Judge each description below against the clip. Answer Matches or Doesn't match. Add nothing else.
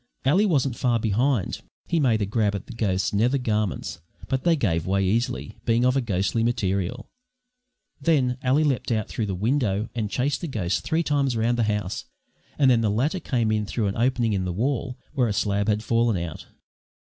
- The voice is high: Doesn't match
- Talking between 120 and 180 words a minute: Doesn't match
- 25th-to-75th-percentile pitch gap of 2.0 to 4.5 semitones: Matches